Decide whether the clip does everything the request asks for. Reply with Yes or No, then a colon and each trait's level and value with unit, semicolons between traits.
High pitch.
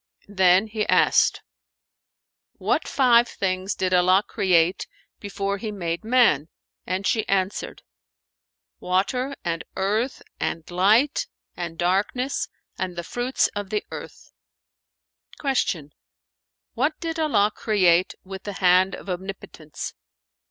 Yes: high, 195 Hz